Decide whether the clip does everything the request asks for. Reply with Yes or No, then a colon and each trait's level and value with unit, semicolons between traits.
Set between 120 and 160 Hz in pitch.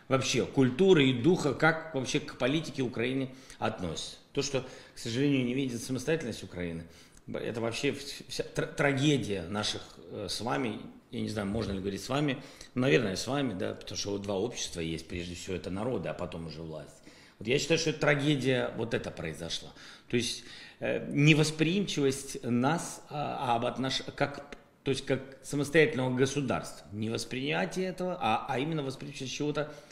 Yes: low, 130 Hz